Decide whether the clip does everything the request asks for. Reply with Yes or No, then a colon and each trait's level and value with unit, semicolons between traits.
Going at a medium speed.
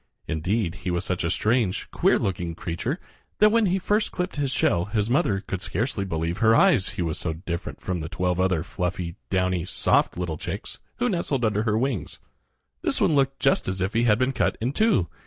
No: fast, 210 wpm